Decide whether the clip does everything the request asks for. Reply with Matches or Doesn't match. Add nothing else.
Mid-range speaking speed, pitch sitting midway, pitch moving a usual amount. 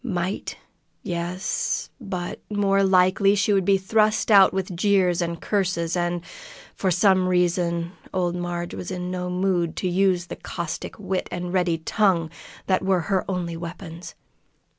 Doesn't match